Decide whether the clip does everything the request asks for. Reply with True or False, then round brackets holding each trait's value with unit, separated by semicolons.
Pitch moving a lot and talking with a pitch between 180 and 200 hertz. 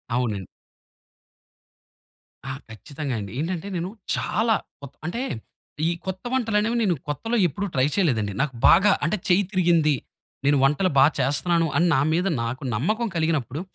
False (6.0 semitones; 165 Hz)